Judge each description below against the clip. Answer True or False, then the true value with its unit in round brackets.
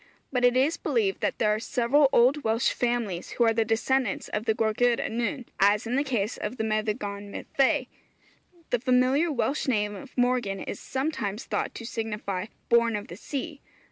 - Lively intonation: False (3.5 semitones)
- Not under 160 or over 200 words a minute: True (180 wpm)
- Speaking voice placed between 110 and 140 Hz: False (235 Hz)